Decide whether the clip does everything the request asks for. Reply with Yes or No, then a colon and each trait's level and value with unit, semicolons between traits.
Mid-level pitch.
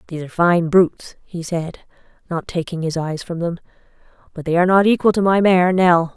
Yes: medium, 175 Hz